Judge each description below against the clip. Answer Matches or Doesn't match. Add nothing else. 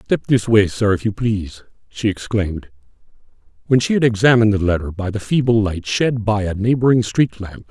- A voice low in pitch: Matches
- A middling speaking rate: Matches